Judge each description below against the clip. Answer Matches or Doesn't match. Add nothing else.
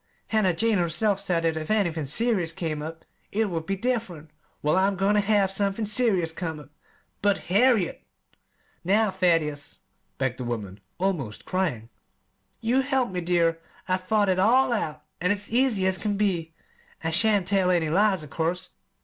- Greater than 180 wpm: Doesn't match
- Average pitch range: Matches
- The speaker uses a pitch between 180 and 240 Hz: Matches